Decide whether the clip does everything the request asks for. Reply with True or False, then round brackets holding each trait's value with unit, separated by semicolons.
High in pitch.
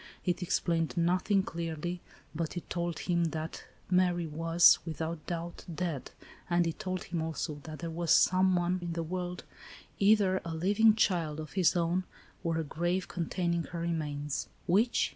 False (170 Hz)